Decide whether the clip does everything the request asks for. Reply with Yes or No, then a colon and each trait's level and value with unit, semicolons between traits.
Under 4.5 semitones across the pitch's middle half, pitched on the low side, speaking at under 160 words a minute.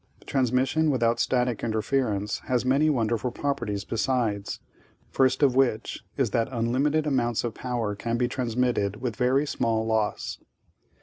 Yes: average, 2.8 semitones; low, 120 Hz; slow, 135 wpm